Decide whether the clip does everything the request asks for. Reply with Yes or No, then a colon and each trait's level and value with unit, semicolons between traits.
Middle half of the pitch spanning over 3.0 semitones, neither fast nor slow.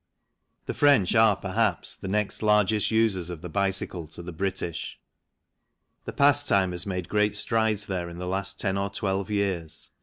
No: average, 2.7 semitones; average, 170 wpm